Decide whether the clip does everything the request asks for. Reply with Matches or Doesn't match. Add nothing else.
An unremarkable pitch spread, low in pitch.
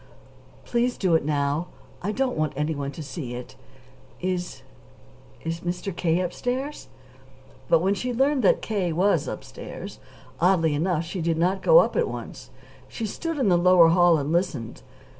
Doesn't match